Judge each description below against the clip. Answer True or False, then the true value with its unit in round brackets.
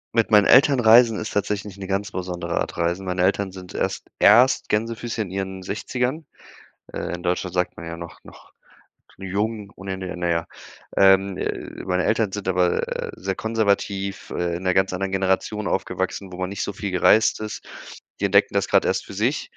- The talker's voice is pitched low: True (95 Hz)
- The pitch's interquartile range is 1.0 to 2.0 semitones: False (2.4 semitones)